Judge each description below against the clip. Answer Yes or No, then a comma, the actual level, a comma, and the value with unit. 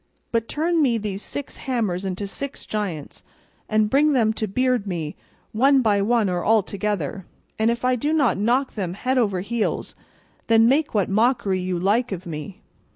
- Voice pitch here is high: Yes, high, 215 Hz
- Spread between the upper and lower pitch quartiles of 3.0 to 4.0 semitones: No, average, 4.5 semitones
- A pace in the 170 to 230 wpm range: Yes, average, 180 wpm